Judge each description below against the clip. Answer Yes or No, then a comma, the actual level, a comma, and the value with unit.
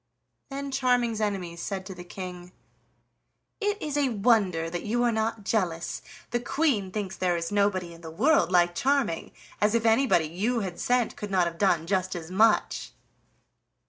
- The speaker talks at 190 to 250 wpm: No, average, 175 wpm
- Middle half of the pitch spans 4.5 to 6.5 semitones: Yes, average, 5.2 semitones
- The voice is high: Yes, high, 200 Hz